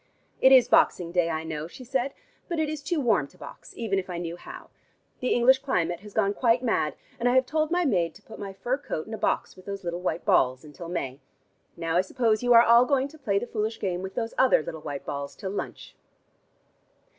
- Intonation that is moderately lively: No, wide, 6.7 semitones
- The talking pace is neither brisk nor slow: No, fast, 235 wpm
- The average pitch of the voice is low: No, high, 205 Hz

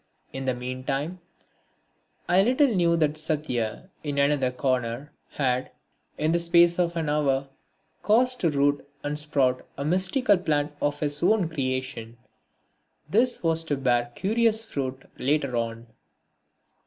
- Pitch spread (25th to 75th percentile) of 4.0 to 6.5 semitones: Yes, average, 4.7 semitones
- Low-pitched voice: No, medium, 150 Hz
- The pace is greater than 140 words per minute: No, slow, 135 wpm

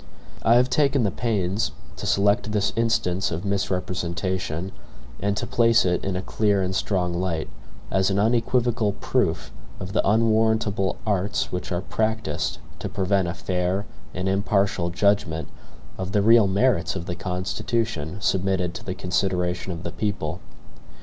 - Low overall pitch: Yes, very low, 95 Hz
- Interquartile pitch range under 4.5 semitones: Yes, average, 3.0 semitones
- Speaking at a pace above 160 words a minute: No, average, 150 wpm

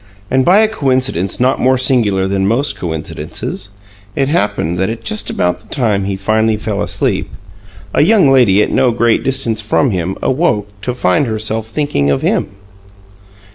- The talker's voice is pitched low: Yes, low, 110 Hz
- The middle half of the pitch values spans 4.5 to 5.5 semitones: Yes, average, 4.9 semitones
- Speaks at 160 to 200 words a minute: Yes, average, 175 wpm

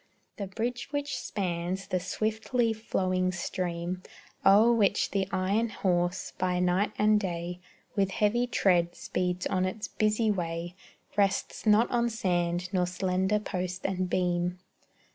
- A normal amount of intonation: Yes, average, 3.0 semitones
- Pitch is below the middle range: No, medium, 185 Hz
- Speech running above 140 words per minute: No, slow, 135 wpm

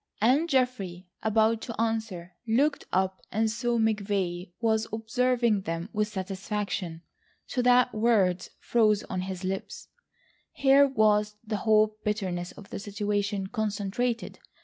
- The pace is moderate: No, slow, 125 wpm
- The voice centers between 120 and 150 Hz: No, high, 215 Hz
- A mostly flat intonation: No, average, 3.0 semitones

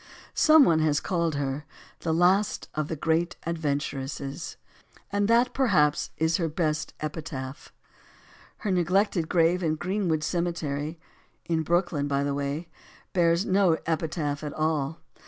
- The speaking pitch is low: No, medium, 160 Hz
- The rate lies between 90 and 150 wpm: Yes, slow, 135 wpm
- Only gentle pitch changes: No, average, 3.0 semitones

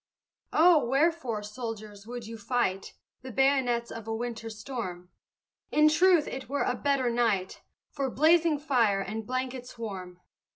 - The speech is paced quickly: No, average, 140 wpm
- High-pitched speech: Yes, high, 245 Hz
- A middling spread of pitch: Yes, average, 4.1 semitones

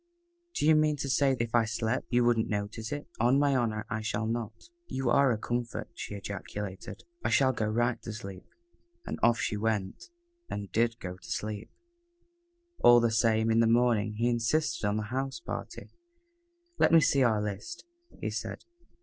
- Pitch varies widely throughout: No, narrow, 2.5 semitones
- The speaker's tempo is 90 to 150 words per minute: No, average, 185 wpm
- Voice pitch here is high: No, low, 115 Hz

